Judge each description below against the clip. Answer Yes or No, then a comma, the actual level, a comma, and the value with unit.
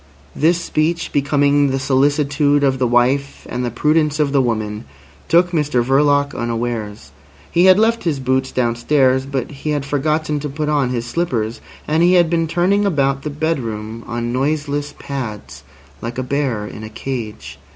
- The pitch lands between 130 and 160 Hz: Yes, medium, 140 Hz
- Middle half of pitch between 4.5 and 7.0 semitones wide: No, average, 3.8 semitones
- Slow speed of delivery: No, average, 170 wpm